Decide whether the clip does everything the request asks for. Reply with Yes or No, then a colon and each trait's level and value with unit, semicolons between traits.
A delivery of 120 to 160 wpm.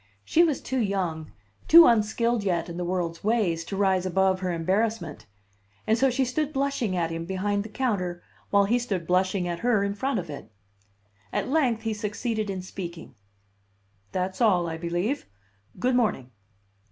No: average, 170 wpm